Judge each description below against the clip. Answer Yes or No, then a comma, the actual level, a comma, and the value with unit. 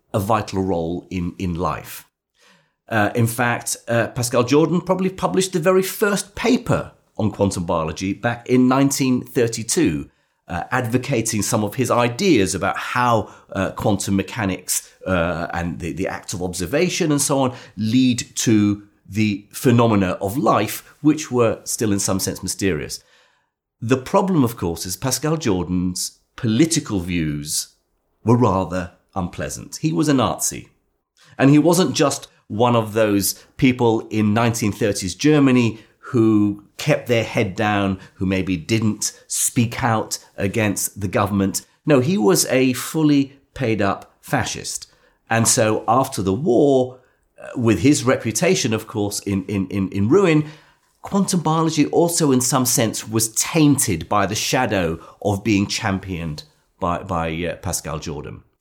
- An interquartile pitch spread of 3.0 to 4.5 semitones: No, average, 5.3 semitones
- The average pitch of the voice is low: Yes, low, 110 Hz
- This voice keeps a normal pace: Yes, average, 145 wpm